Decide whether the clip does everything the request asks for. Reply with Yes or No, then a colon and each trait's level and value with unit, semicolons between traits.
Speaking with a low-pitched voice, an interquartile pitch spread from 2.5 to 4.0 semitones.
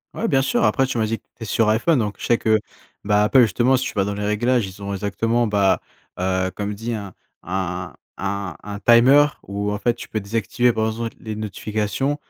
Yes: low, 110 Hz; average, 2.9 semitones